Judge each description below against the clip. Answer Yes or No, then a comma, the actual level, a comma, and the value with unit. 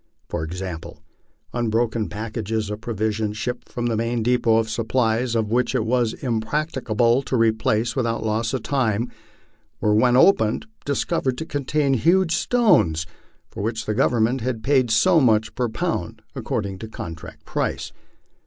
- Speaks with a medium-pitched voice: No, low, 115 Hz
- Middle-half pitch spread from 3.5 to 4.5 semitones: No, narrow, 2.6 semitones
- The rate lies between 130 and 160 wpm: Yes, average, 150 wpm